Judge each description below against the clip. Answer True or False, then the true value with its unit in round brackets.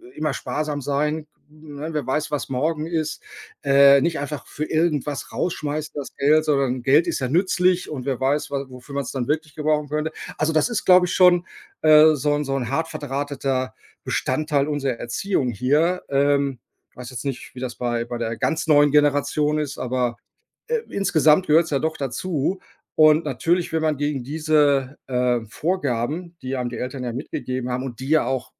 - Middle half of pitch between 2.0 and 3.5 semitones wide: True (2.9 semitones)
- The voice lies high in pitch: False (145 Hz)